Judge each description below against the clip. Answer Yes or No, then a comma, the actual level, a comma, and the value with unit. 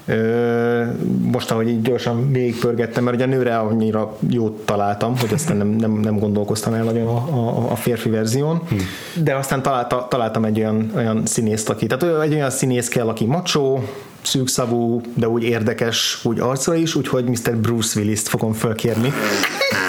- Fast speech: Yes, fast, 165 wpm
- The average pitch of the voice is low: Yes, low, 120 Hz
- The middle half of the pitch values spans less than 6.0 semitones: Yes, narrow, 2.4 semitones